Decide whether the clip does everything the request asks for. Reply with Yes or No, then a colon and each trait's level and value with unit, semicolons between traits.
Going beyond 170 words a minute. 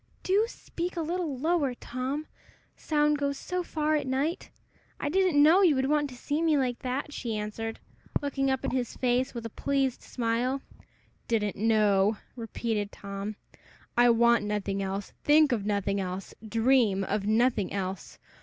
No: average, 165 wpm